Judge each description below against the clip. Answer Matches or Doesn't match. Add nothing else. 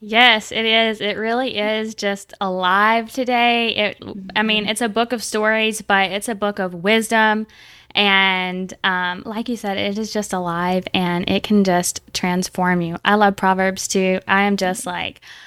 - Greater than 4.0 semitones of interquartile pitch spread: Doesn't match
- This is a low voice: Doesn't match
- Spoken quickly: Doesn't match